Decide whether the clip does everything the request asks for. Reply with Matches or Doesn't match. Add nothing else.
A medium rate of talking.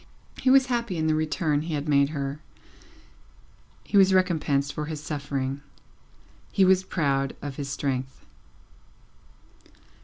Doesn't match